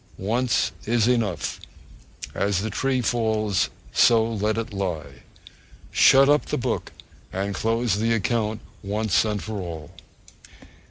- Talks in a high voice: No, low, 110 Hz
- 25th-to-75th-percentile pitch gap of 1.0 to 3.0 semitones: Yes, average, 2.7 semitones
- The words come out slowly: Yes, slow, 120 wpm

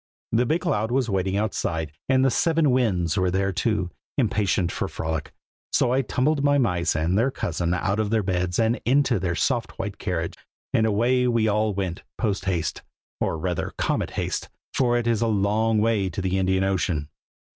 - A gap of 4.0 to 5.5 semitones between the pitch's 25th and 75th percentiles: Yes, average, 4.5 semitones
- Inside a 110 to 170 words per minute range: No, average, 195 wpm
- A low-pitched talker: Yes, low, 105 Hz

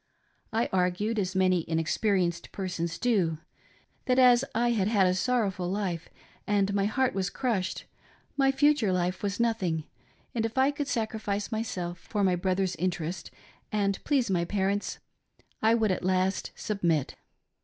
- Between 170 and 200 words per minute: No, average, 150 wpm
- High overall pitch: Yes, high, 195 Hz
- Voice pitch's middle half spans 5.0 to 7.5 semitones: No, average, 3.7 semitones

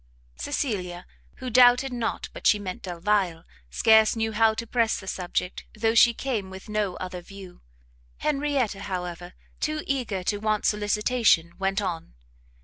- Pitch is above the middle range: Yes, high, 210 Hz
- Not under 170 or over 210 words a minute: No, average, 145 wpm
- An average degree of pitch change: Yes, average, 4.0 semitones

